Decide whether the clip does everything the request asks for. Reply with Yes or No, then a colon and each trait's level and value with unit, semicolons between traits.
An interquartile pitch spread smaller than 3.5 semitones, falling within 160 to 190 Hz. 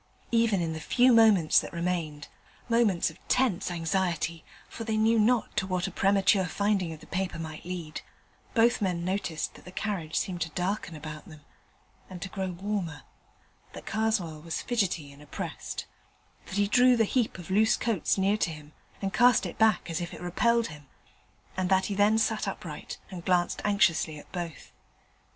No: average, 4.3 semitones; medium, 185 Hz